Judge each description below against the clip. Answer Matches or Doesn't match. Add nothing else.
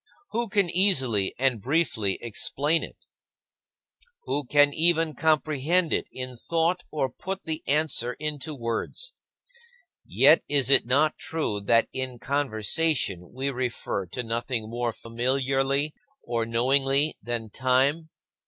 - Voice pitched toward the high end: Doesn't match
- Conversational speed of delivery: Doesn't match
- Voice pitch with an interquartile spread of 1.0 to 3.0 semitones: Doesn't match